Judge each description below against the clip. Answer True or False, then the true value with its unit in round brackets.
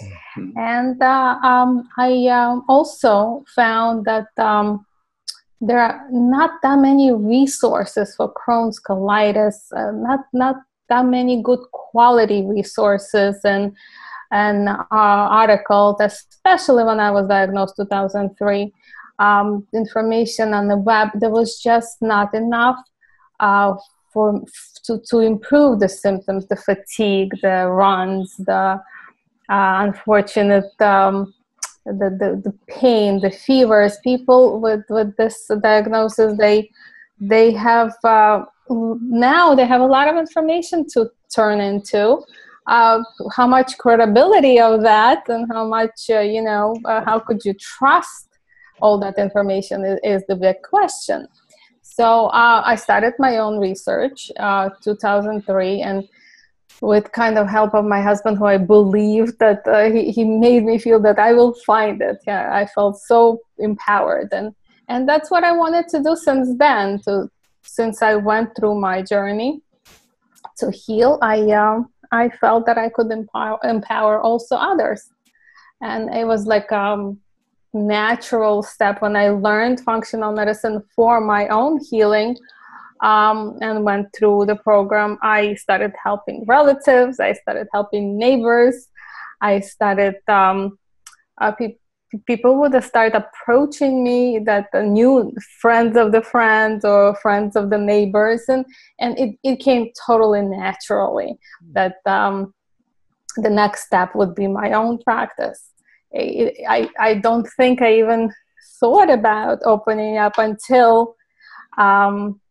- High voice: True (220 Hz)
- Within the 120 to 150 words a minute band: True (145 wpm)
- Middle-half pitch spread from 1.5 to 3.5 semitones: True (3.1 semitones)